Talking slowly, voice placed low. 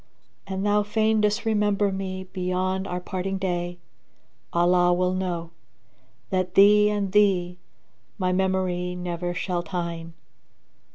No: slow, 120 wpm; medium, 185 Hz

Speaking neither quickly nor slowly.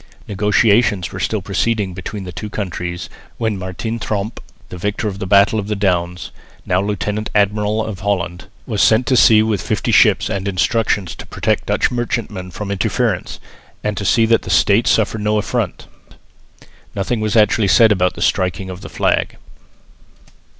Yes: average, 170 wpm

